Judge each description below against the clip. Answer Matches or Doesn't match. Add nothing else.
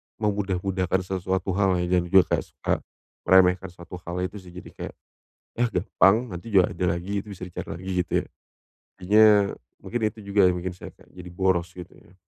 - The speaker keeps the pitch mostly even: Matches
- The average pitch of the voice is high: Doesn't match